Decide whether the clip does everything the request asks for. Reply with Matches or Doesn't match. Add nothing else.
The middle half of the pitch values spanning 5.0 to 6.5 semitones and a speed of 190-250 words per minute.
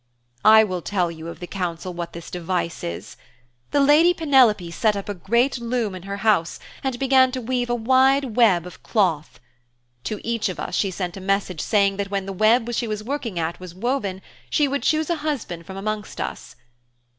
Matches